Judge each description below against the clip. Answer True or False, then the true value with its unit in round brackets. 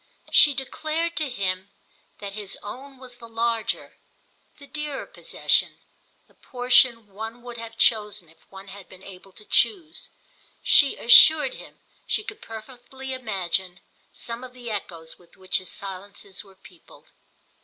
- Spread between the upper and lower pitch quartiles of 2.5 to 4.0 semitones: False (5.0 semitones)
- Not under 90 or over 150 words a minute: True (145 wpm)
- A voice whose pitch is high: True (225 Hz)